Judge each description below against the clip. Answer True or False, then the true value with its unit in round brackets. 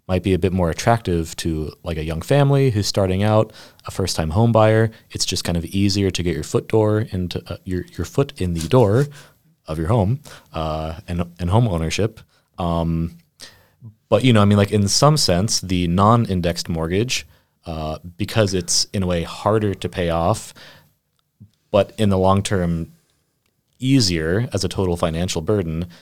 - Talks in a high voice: False (95 Hz)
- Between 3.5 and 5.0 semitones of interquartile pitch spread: True (4.3 semitones)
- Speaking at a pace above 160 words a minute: True (180 wpm)